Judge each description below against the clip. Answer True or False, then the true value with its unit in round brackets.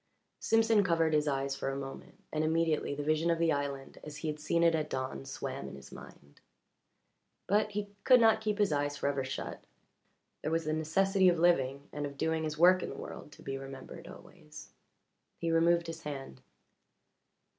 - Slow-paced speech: False (190 wpm)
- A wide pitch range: False (3.3 semitones)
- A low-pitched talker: False (155 Hz)